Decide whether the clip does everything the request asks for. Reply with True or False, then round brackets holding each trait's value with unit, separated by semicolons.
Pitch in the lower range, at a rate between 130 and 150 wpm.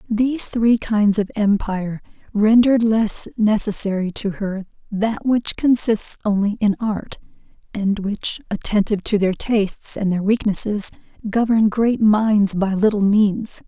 False (210 Hz; 135 wpm)